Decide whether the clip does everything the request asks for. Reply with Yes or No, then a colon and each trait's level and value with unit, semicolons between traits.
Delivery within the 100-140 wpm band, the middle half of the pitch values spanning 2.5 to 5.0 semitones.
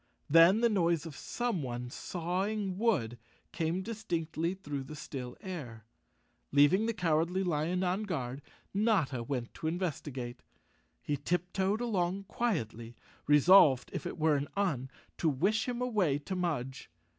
No: slow, 135 wpm; wide, 5.5 semitones